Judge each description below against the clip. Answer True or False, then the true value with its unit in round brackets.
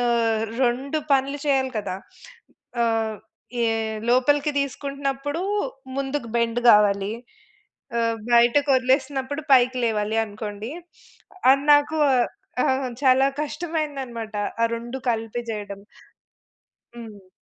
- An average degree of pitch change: True (3.6 semitones)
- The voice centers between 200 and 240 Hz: False (250 Hz)